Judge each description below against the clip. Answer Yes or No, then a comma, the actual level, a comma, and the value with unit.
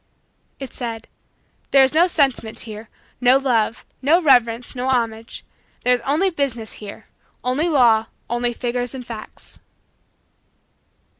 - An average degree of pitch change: Yes, average, 3.0 semitones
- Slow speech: Yes, slow, 130 wpm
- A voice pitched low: No, high, 245 Hz